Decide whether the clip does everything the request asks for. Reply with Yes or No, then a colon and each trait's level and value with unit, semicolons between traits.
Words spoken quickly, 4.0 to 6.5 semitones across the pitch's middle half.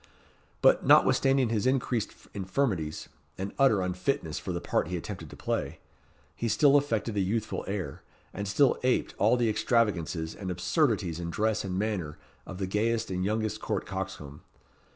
No: average, 160 wpm; average, 4.3 semitones